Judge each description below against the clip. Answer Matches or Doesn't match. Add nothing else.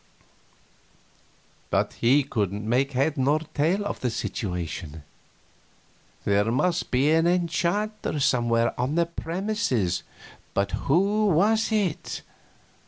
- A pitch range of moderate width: Doesn't match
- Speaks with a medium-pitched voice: Matches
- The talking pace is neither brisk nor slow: Doesn't match